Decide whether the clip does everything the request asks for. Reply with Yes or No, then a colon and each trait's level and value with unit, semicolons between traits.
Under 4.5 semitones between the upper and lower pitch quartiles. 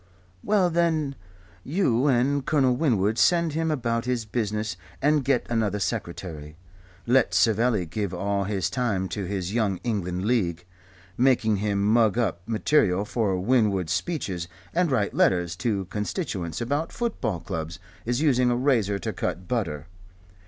No: average, 5.2 semitones